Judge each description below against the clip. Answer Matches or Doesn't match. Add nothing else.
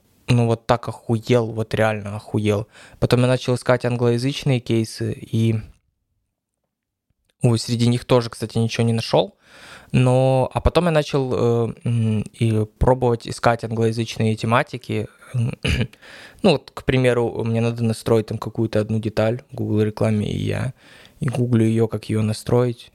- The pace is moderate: Matches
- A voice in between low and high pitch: Doesn't match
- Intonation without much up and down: Matches